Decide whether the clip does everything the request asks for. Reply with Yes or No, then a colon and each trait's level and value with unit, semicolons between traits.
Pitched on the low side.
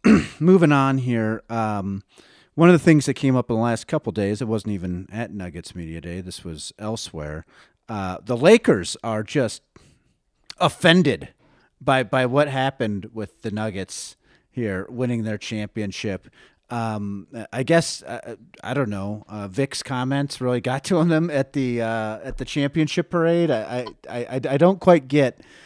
Yes: low, 120 Hz